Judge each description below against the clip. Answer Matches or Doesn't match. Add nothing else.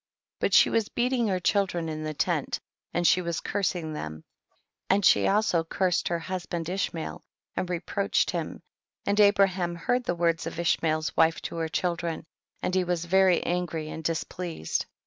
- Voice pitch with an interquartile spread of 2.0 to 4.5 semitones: Matches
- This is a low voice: Doesn't match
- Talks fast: Doesn't match